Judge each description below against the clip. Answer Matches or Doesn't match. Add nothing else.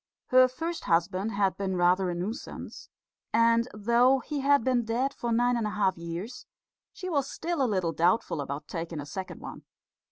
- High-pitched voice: Matches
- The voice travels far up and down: Matches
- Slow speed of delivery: Doesn't match